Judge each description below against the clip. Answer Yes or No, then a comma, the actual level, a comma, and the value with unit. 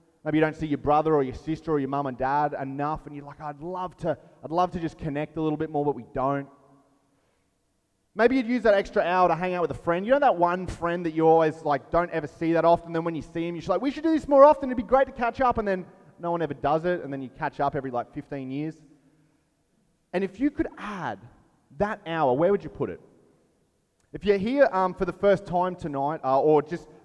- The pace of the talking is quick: Yes, fast, 260 wpm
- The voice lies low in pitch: No, medium, 160 Hz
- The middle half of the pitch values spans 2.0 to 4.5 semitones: Yes, average, 4.2 semitones